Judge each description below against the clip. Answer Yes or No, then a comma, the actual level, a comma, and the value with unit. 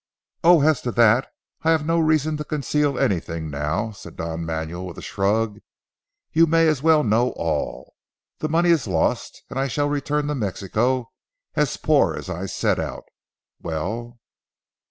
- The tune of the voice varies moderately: No, wide, 8.4 semitones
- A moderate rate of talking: Yes, average, 165 wpm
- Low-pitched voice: Yes, low, 120 Hz